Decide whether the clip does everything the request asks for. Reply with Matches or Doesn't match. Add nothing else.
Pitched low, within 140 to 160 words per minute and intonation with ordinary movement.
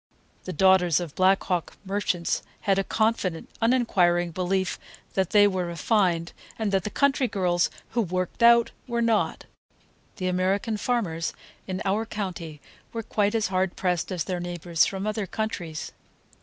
Doesn't match